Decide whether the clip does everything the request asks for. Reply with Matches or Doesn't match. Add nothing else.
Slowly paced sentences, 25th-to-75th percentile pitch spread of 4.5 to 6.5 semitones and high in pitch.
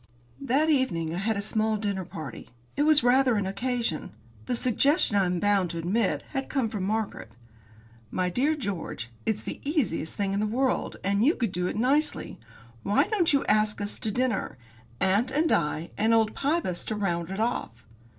Doesn't match